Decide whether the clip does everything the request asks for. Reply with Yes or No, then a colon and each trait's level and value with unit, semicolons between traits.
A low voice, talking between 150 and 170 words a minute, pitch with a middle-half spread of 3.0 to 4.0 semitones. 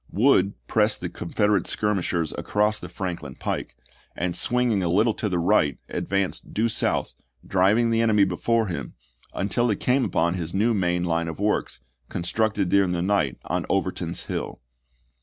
Yes: very low, 95 Hz; average, 165 wpm; average, 3.6 semitones